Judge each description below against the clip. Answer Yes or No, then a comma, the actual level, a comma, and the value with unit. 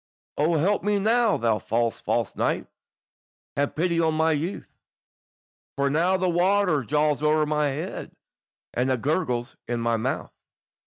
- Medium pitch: Yes, medium, 155 Hz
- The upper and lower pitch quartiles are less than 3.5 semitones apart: No, average, 5.0 semitones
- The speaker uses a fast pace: No, average, 150 wpm